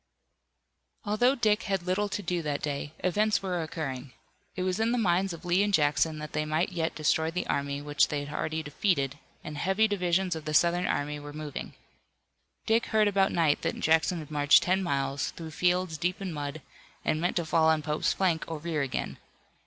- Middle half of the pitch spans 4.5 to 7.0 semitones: No, average, 3.8 semitones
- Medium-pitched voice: Yes, medium, 165 Hz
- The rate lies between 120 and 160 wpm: No, average, 200 wpm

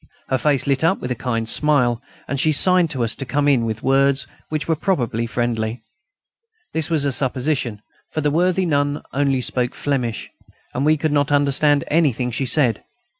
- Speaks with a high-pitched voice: No, medium, 140 Hz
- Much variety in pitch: No, average, 3.5 semitones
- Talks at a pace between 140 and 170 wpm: No, average, 185 wpm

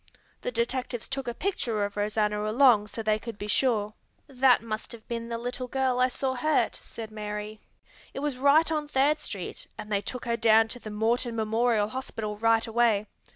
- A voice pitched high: Yes, high, 230 Hz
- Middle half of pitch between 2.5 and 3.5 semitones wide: Yes, average, 3.0 semitones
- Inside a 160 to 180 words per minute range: No, average, 195 wpm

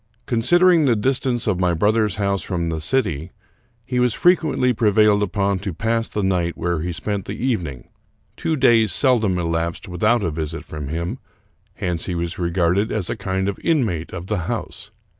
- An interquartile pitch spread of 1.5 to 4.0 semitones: No, average, 5.1 semitones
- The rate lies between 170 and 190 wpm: Yes, average, 180 wpm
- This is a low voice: Yes, low, 100 Hz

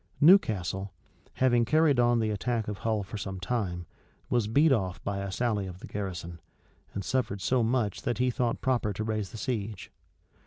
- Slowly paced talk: No, average, 190 wpm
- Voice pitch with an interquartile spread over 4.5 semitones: No, average, 3.8 semitones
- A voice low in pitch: Yes, low, 110 Hz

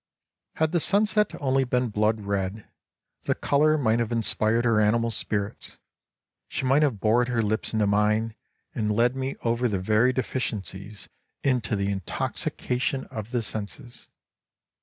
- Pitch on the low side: Yes, low, 115 Hz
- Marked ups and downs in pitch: No, average, 3.3 semitones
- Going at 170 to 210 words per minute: No, average, 150 wpm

